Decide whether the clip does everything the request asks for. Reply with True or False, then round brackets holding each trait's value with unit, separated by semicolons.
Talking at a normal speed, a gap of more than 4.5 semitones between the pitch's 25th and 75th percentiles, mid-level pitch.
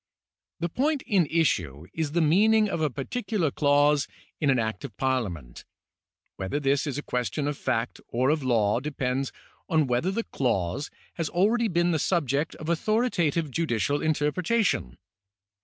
True (155 wpm; 5.2 semitones; 150 Hz)